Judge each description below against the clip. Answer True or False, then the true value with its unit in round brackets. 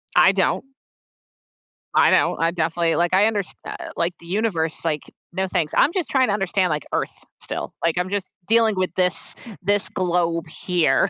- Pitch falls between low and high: True (180 Hz)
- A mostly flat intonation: False (3.2 semitones)